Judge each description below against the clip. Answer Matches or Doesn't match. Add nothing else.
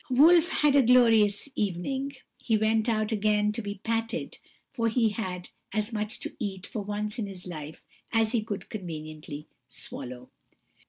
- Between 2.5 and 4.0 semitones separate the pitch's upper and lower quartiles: Matches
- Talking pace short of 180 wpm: Matches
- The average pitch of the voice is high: Matches